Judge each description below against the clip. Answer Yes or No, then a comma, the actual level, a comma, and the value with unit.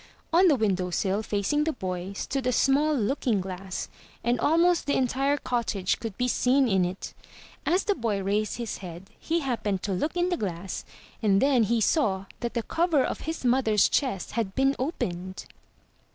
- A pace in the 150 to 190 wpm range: Yes, average, 180 wpm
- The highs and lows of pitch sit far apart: Yes, wide, 6.2 semitones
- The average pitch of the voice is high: Yes, high, 235 Hz